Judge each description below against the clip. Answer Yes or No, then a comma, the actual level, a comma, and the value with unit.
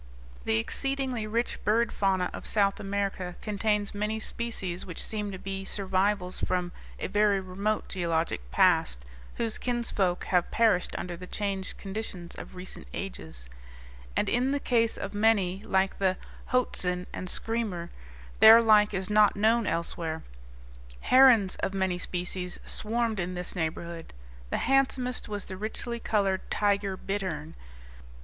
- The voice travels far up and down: No, average, 3.3 semitones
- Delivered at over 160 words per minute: No, average, 140 wpm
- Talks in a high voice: Yes, high, 195 Hz